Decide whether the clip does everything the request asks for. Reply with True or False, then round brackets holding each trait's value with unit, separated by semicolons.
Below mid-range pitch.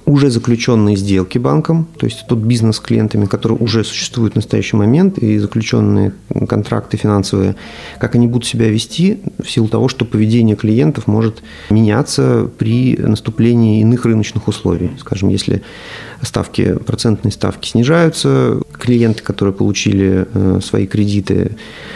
True (115 Hz)